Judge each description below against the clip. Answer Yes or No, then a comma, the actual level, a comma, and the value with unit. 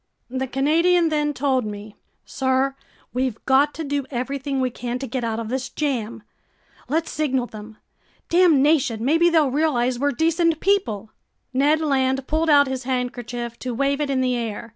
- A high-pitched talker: Yes, very high, 265 Hz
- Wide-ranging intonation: No, average, 3.5 semitones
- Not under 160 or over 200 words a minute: Yes, average, 165 wpm